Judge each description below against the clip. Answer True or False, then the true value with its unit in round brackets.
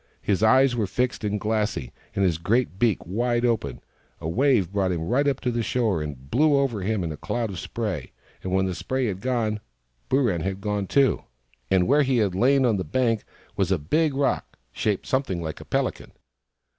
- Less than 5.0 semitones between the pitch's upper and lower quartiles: False (5.3 semitones)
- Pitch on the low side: True (110 Hz)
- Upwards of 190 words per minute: True (200 wpm)